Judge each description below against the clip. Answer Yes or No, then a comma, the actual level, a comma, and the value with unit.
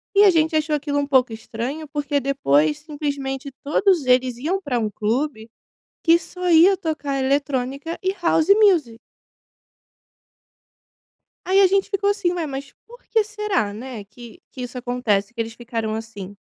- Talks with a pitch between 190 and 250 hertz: No, very high, 280 Hz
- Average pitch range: No, wide, 6.1 semitones